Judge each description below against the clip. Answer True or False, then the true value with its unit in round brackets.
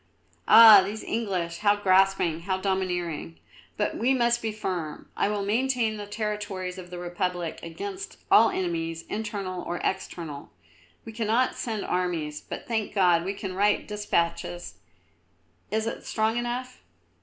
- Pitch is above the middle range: True (195 Hz)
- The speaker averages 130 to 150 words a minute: True (145 wpm)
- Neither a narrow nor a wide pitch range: True (3.7 semitones)